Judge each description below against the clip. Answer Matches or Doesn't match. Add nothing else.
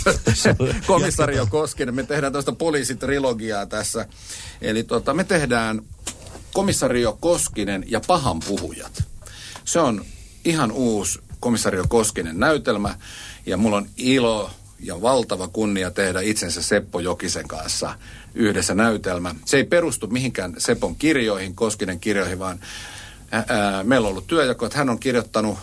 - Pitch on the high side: Doesn't match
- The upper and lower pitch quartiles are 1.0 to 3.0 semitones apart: Doesn't match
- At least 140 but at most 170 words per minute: Doesn't match